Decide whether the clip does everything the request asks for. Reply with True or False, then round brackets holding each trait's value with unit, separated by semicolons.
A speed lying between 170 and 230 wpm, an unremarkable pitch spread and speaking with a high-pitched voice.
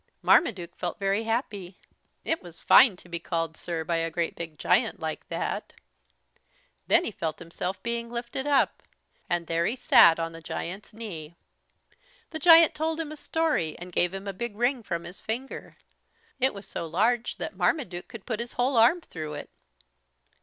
False (180 wpm; 6.3 semitones; 195 Hz)